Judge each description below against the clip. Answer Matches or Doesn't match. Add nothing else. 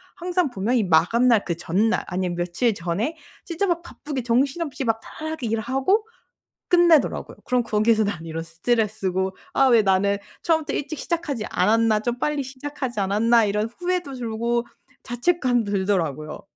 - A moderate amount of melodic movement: Doesn't match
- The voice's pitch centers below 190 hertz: Doesn't match